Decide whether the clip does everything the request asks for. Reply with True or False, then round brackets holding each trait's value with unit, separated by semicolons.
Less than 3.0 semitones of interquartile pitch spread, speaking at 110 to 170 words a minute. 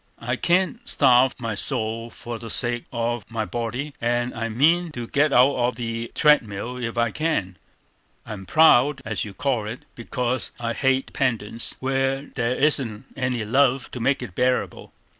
True (2.6 semitones; 165 wpm)